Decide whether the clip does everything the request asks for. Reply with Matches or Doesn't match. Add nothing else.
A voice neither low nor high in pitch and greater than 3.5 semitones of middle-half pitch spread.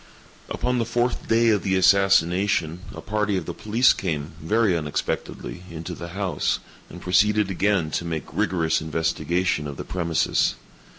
Doesn't match